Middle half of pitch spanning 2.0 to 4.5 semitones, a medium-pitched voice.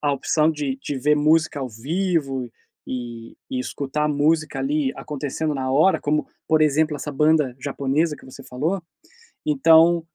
Yes: average, 2.7 semitones; medium, 150 Hz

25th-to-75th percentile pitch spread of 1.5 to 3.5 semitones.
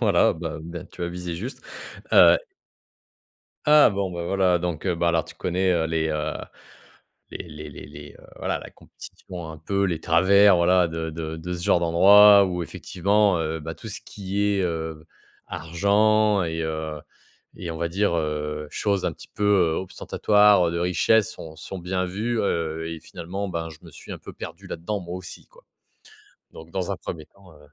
Yes: average, 3.2 semitones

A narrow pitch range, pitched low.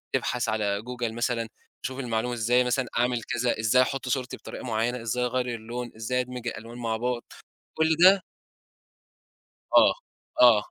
Yes: narrow, 1.7 semitones; low, 120 Hz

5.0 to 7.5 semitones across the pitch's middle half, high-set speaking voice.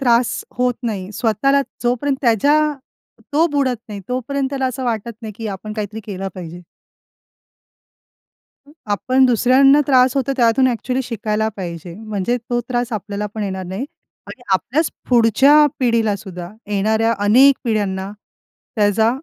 No: average, 3.8 semitones; high, 230 Hz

